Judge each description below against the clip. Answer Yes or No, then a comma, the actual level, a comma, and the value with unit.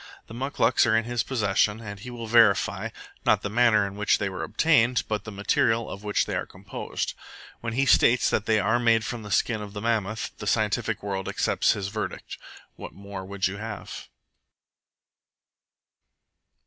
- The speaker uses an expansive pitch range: No, narrow, 2.5 semitones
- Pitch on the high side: No, low, 110 Hz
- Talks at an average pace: Yes, average, 180 wpm